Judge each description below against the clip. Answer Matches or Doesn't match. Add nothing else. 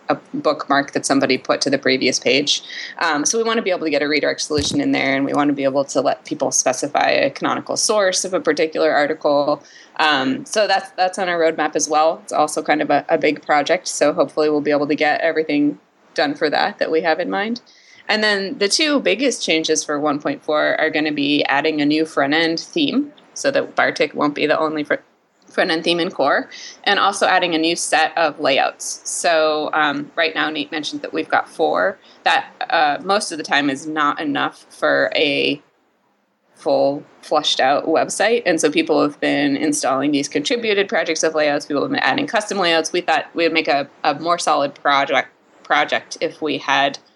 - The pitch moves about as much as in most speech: Matches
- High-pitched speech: Doesn't match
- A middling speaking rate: Doesn't match